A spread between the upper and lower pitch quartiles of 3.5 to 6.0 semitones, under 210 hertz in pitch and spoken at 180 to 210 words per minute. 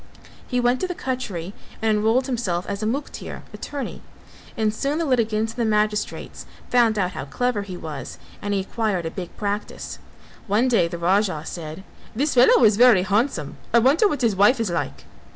No: average, 4.5 semitones; high, 215 Hz; average, 190 wpm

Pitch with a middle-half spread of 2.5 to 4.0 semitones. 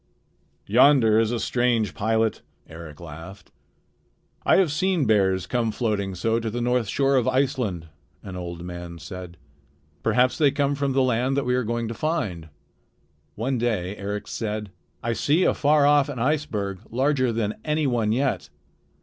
No: average, 5.1 semitones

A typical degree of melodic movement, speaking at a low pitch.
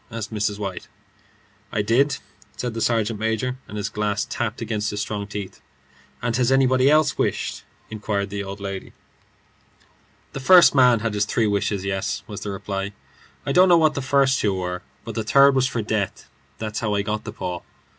Yes: average, 3.7 semitones; low, 110 Hz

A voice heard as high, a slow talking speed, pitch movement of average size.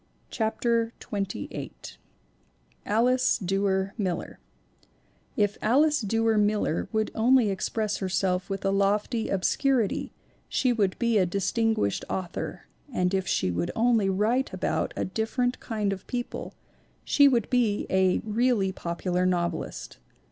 Yes: high, 210 Hz; slow, 130 wpm; average, 3.5 semitones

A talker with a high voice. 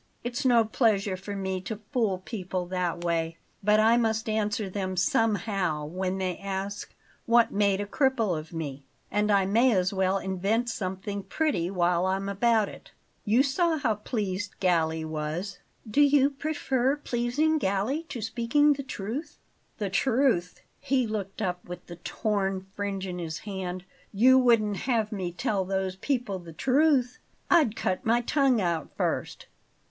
Yes: high, 205 Hz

